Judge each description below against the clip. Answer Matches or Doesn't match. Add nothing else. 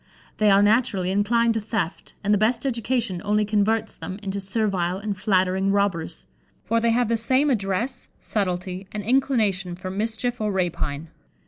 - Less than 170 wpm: Matches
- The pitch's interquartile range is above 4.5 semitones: Doesn't match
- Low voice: Doesn't match